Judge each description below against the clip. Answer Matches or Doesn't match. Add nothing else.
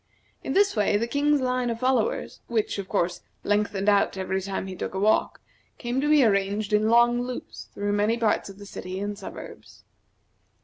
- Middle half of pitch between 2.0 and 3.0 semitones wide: Doesn't match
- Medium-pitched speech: Doesn't match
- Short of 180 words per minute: Doesn't match